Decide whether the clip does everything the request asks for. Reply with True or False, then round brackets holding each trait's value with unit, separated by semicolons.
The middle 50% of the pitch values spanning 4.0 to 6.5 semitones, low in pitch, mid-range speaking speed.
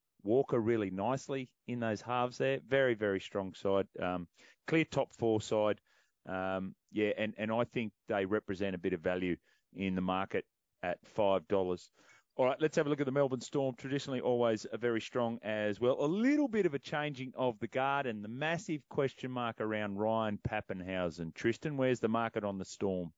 True (5.1 semitones; 115 Hz; 190 wpm)